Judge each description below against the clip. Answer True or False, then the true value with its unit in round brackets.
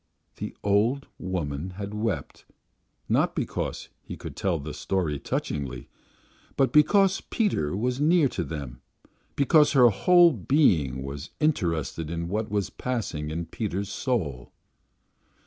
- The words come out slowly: True (130 wpm)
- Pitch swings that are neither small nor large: False (9.0 semitones)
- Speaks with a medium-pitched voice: False (100 Hz)